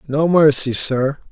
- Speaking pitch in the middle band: Yes, medium, 145 Hz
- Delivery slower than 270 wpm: Yes, slow, 135 wpm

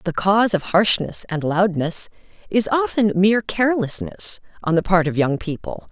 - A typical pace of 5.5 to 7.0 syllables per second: No, 4.9 syllables/s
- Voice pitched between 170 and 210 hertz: Yes, medium, 185 Hz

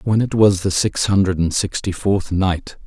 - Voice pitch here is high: No, very low, 95 Hz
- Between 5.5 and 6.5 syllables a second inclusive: No, 4.4 syllables/s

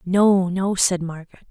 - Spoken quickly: No, average, 160 wpm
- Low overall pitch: No, medium, 185 Hz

